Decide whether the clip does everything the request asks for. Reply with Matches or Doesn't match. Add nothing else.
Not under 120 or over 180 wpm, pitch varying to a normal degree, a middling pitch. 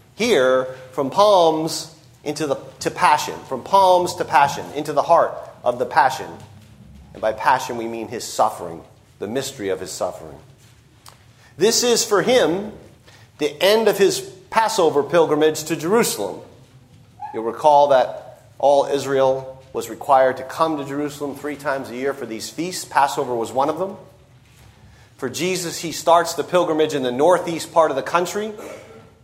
Matches